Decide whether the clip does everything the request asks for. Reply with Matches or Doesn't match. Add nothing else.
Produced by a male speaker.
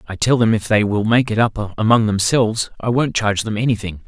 Matches